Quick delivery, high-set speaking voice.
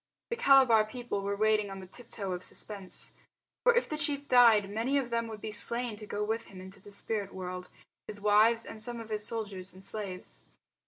Yes: fast, 215 wpm; high, 215 Hz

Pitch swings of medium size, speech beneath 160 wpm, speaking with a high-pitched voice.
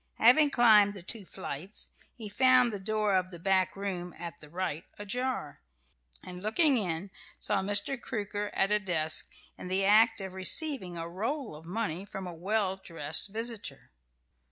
No: average, 3.6 semitones; average, 165 wpm; high, 195 Hz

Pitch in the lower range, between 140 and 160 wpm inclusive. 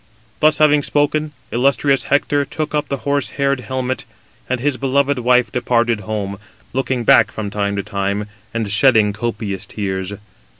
Yes: low, 125 Hz; average, 155 wpm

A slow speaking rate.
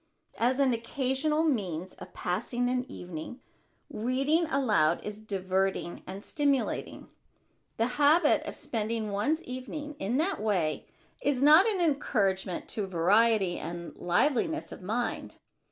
Yes: slow, 125 wpm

